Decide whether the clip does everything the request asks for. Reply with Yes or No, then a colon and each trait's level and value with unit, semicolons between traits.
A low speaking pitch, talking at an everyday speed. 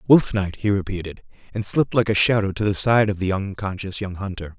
No: low, 100 Hz; fast, 220 wpm